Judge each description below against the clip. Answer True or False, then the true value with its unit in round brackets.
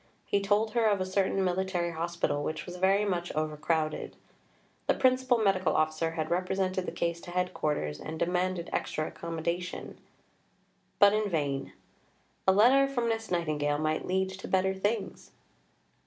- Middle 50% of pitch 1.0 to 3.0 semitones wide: False (3.4 semitones)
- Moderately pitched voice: True (180 Hz)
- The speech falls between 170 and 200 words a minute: False (150 wpm)